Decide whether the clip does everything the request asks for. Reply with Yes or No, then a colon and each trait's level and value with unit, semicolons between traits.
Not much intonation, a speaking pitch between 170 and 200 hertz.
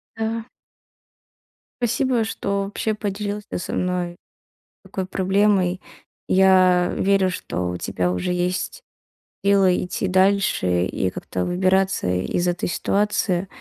Yes: narrow, 2.2 semitones; high, 190 Hz